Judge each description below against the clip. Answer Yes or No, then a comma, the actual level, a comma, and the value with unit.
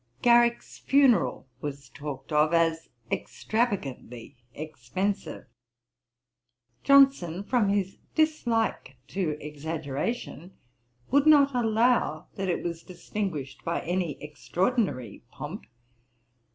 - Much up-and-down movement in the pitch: Yes, wide, 7.8 semitones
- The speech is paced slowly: Yes, slow, 90 wpm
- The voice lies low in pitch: No, medium, 180 Hz